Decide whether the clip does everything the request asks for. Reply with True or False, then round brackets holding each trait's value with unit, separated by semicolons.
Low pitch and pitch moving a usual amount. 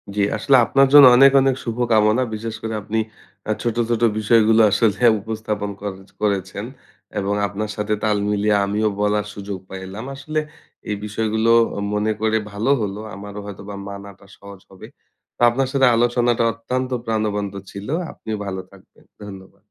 False (105 Hz; 2.2 semitones)